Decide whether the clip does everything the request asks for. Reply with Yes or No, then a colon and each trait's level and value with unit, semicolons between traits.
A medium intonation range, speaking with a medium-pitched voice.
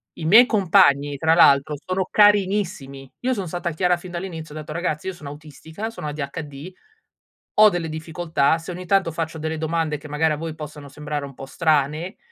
Yes: average, 3.0 semitones; medium, 160 Hz